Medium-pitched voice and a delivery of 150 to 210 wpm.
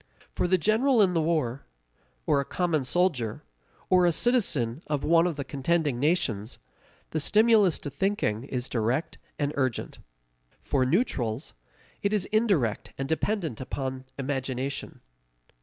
No: medium, 150 Hz; average, 140 wpm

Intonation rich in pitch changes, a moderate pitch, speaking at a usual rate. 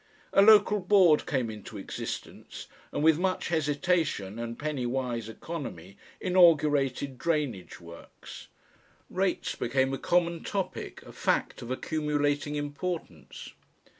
No: wide, 5.7 semitones; medium, 145 Hz; slow, 115 wpm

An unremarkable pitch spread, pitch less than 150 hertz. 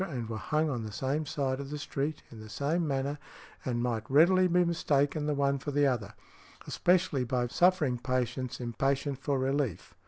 Yes: average, 3.1 semitones; medium, 140 Hz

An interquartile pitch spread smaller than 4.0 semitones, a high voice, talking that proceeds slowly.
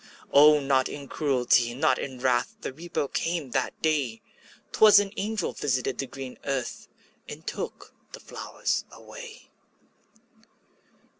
No: average, 3.6 semitones; medium, 140 Hz; slow, 130 wpm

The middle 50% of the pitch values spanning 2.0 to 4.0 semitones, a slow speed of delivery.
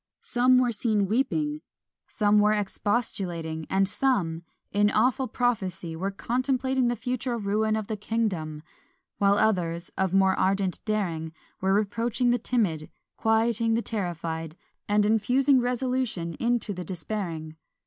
No: average, 4.6 semitones; slow, 130 wpm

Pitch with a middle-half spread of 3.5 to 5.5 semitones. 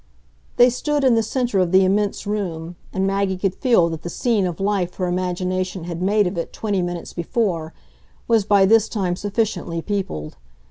No: average, 3.0 semitones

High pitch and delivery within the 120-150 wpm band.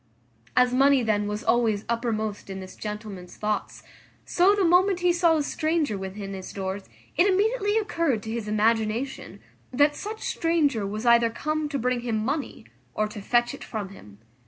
No: high, 235 Hz; average, 175 wpm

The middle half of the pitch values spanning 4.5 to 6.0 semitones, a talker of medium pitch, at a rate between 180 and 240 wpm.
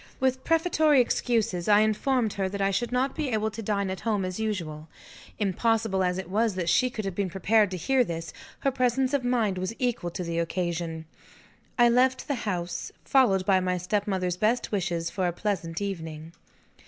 No: average, 4.9 semitones; high, 205 Hz; average, 190 wpm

